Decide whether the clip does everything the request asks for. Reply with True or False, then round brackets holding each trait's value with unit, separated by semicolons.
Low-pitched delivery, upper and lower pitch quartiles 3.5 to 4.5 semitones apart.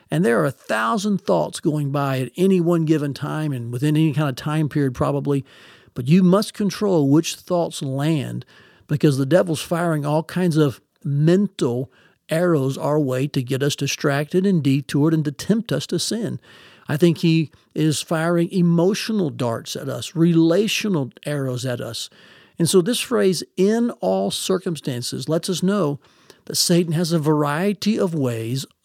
False (155 Hz; 4.1 semitones)